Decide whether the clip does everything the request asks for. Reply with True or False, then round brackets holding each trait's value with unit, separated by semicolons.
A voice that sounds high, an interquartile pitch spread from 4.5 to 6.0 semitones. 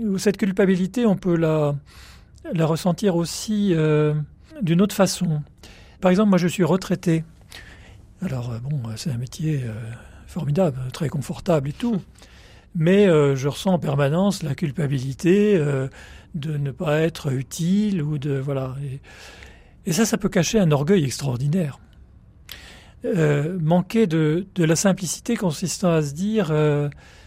False (160 Hz; 5.1 semitones)